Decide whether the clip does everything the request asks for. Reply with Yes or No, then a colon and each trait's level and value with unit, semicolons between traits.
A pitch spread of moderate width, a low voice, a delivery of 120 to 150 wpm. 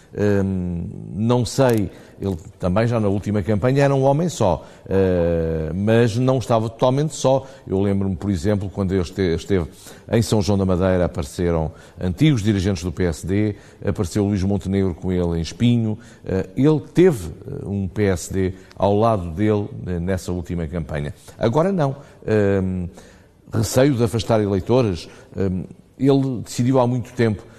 Yes: average, 4.2 semitones; low, 100 Hz; average, 145 wpm